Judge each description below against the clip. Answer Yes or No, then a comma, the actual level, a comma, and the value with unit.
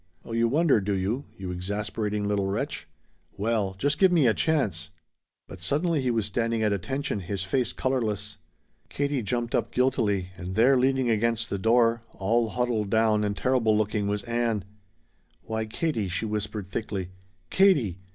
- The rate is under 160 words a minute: No, average, 165 wpm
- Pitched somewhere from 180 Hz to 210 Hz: No, low, 110 Hz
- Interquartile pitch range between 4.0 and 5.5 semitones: No, average, 3.5 semitones